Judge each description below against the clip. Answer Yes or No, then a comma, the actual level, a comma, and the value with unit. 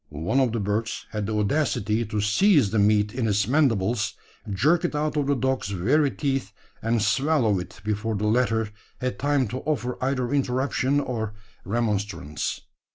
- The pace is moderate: Yes, average, 165 wpm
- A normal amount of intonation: Yes, average, 4.6 semitones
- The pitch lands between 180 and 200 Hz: No, low, 115 Hz